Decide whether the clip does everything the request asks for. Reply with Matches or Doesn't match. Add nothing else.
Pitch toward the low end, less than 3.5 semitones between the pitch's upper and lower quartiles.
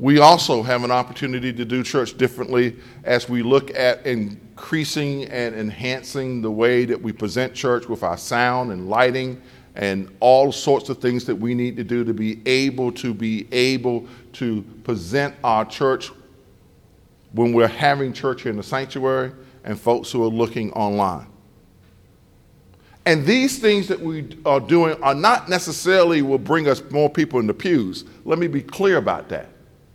Matches